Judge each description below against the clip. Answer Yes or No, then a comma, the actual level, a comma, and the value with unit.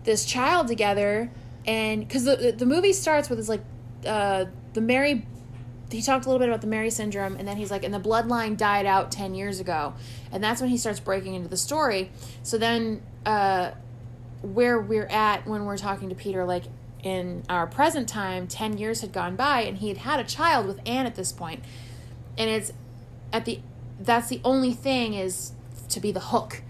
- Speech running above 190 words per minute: Yes, average, 200 wpm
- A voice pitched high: Yes, high, 200 Hz